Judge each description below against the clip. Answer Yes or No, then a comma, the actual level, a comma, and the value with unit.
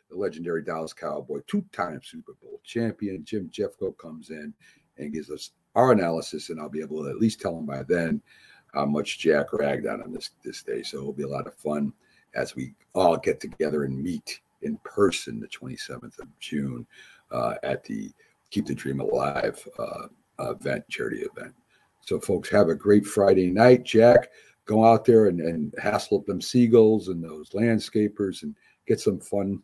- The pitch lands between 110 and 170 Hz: No, very low, 95 Hz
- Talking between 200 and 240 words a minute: No, average, 185 wpm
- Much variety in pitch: Yes, wide, 6.8 semitones